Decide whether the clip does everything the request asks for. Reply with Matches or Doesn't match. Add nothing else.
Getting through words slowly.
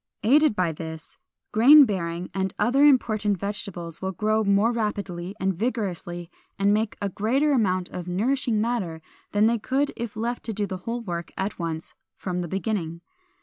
Doesn't match